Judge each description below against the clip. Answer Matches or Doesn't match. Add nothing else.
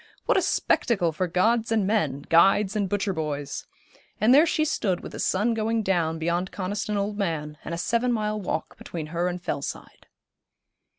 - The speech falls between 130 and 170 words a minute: Doesn't match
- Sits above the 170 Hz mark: Matches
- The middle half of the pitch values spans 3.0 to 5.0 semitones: Matches